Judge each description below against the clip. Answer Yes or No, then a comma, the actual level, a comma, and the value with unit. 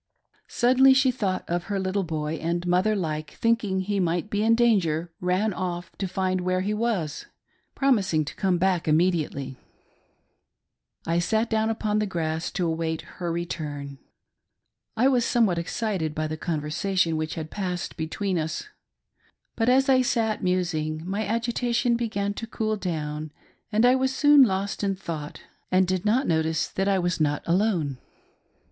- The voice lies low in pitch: No, medium, 185 Hz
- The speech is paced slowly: No, average, 160 wpm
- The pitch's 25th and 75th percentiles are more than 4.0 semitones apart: Yes, average, 5.0 semitones